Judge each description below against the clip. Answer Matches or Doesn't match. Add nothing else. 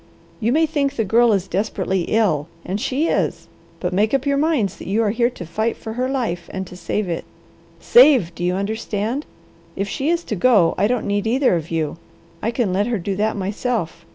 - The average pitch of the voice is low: Doesn't match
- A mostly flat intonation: Doesn't match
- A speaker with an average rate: Doesn't match